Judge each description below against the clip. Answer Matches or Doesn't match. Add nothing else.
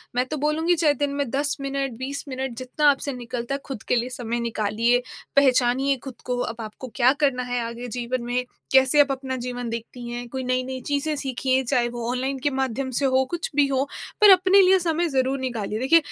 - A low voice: Doesn't match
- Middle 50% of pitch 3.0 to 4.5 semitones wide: Doesn't match